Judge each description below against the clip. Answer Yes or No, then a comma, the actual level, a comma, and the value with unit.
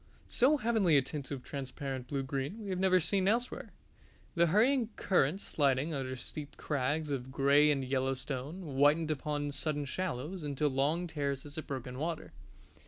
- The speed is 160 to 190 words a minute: Yes, average, 165 wpm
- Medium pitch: Yes, medium, 145 Hz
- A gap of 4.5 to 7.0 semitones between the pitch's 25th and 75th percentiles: No, average, 4.1 semitones